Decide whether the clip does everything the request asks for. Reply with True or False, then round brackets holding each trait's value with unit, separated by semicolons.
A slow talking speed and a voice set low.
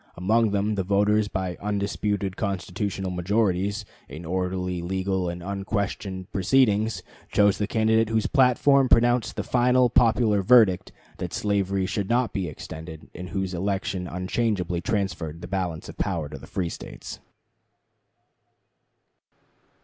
True (130 wpm; 100 Hz)